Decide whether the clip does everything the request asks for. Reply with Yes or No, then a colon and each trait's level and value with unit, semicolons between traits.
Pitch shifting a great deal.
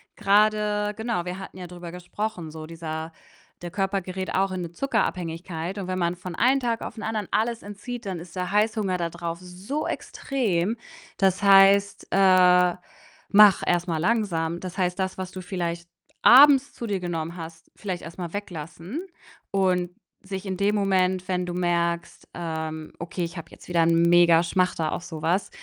No: average, 2.8 semitones